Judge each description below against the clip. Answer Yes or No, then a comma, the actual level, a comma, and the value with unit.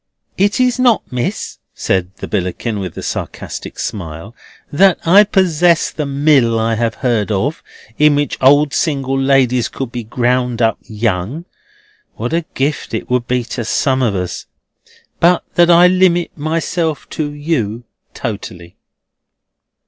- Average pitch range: No, wide, 6.1 semitones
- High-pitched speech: No, low, 130 Hz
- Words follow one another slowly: No, average, 145 wpm